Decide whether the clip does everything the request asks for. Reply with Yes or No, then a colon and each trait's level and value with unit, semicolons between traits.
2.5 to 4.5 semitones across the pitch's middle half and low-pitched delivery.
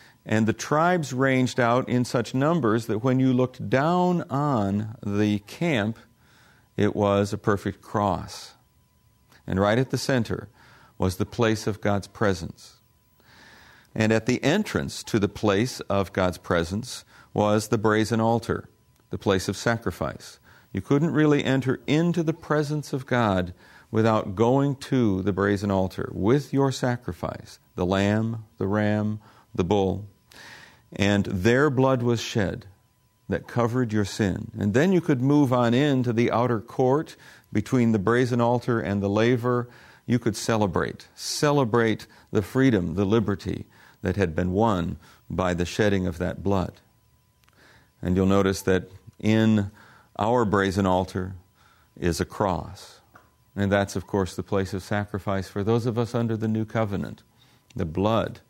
Yes: average, 3.8 semitones; low, 110 Hz